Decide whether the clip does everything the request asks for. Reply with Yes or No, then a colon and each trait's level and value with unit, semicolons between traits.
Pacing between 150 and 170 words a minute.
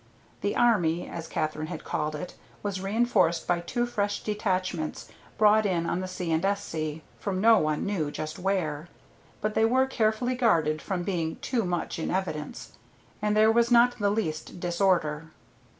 Yes: average, 165 wpm